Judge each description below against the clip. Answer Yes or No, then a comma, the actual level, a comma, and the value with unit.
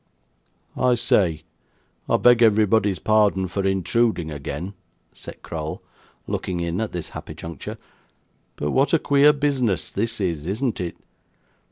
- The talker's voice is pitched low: Yes, low, 100 Hz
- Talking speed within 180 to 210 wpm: No, slow, 135 wpm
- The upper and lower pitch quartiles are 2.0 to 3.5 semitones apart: No, wide, 5.5 semitones